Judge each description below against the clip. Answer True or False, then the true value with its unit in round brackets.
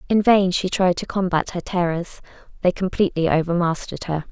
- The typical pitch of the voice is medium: True (180 Hz)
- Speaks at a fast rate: False (155 wpm)